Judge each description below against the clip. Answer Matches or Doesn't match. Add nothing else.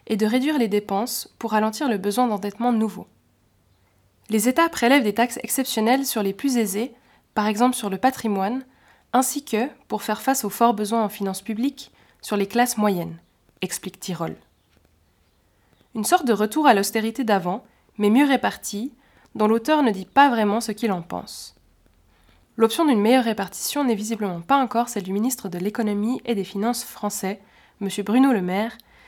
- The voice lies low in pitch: Doesn't match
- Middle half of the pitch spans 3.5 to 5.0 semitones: Matches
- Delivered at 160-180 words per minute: Matches